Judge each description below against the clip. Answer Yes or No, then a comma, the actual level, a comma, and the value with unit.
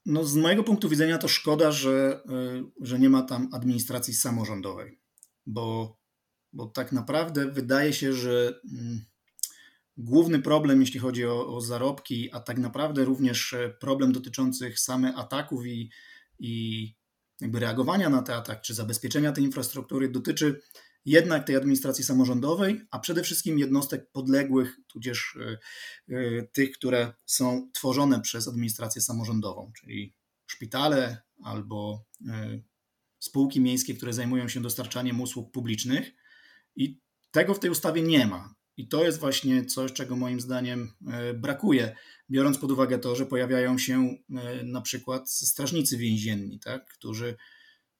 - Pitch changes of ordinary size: No, narrow, 2.2 semitones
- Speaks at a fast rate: No, average, 130 wpm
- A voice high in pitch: No, low, 130 Hz